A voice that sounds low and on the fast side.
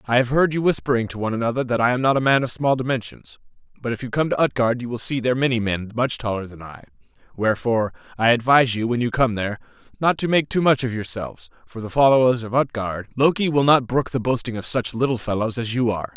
Yes: low, 125 Hz; fast, 245 wpm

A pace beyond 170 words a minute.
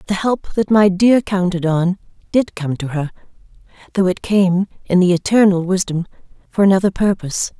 No: average, 165 wpm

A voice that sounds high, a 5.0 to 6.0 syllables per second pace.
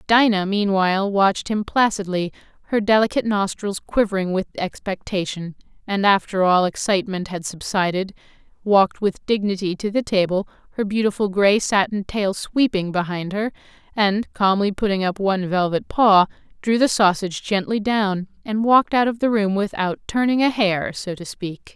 Yes: high, 200 Hz; 5.1 syllables/s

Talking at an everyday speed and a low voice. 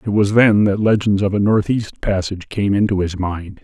No: fast, 215 wpm; low, 100 Hz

